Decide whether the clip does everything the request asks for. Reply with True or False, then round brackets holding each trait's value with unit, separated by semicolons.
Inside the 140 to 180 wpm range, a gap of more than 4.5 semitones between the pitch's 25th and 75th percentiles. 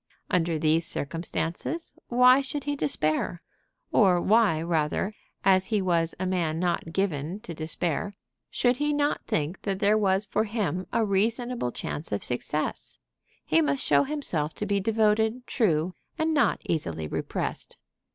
True (150 wpm; 5.6 semitones)